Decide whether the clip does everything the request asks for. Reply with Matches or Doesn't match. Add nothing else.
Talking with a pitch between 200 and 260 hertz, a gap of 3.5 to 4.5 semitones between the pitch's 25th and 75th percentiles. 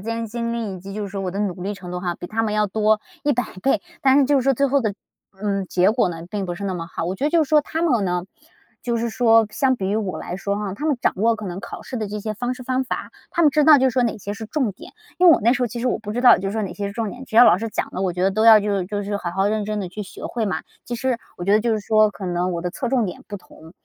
Matches